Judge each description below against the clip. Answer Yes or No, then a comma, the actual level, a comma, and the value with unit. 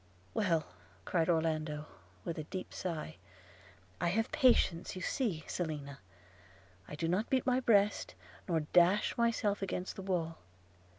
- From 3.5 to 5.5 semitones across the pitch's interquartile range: Yes, average, 4.6 semitones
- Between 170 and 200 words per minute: No, average, 140 wpm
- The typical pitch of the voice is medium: Yes, medium, 175 Hz